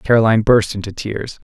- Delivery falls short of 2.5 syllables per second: No, 5.8 syllables/s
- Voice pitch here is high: No, low, 110 Hz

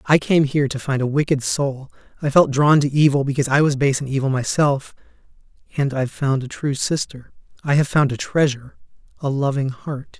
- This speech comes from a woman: No, male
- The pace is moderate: Yes, average, 190 wpm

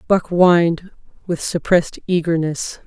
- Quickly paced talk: No, slow, 105 wpm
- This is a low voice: No, medium, 170 Hz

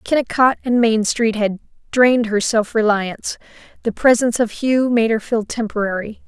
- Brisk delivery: No, average, 165 wpm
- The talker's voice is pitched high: Yes, high, 225 Hz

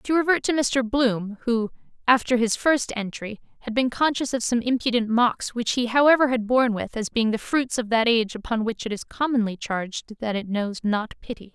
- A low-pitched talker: No, high, 235 Hz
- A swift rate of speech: Yes, fast, 215 wpm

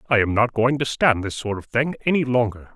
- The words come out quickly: Yes, fast, 260 wpm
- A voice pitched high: No, low, 120 Hz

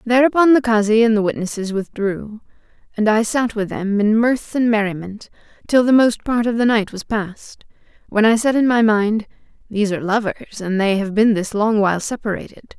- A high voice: Yes, high, 220 Hz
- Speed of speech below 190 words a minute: No, average, 195 wpm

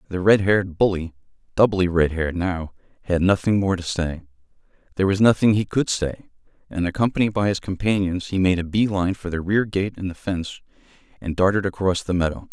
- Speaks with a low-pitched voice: Yes, very low, 95 Hz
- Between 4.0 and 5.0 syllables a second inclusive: No, 5.9 syllables/s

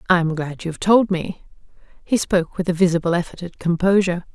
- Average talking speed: Yes, average, 180 wpm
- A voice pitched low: No, medium, 180 Hz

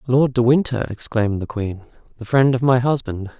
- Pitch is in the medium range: No, low, 120 Hz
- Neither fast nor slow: Yes, average, 195 wpm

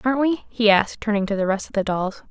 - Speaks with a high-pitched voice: Yes, high, 215 Hz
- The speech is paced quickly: Yes, fast, 285 wpm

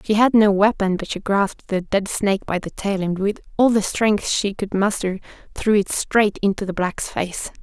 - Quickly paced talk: Yes, fast, 220 wpm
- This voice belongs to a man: No, female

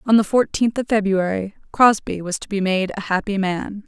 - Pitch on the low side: No, high, 205 Hz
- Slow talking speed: No, average, 200 wpm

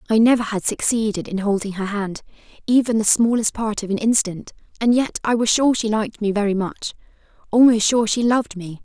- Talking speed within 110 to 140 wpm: No, fast, 205 wpm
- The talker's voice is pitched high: Yes, high, 215 Hz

